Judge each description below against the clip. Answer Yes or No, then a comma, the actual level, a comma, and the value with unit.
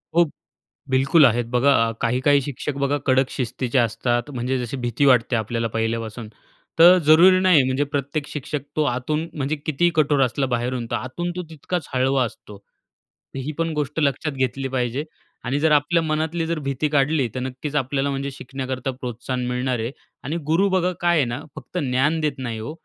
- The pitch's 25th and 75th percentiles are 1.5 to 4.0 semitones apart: Yes, average, 3.4 semitones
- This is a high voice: No, low, 135 Hz